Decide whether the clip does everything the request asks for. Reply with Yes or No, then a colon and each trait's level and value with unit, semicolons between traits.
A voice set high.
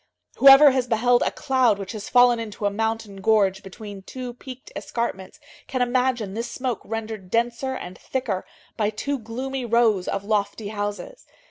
Yes: high, 225 Hz